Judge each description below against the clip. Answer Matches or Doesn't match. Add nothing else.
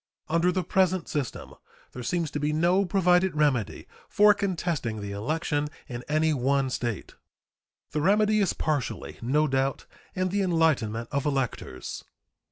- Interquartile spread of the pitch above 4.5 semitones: Matches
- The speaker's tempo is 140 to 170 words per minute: Matches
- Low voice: Doesn't match